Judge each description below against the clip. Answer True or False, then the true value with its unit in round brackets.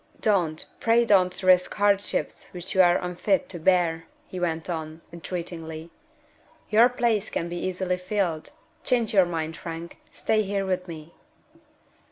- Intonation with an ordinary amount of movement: True (3.1 semitones)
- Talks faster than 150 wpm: False (145 wpm)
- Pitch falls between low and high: True (180 Hz)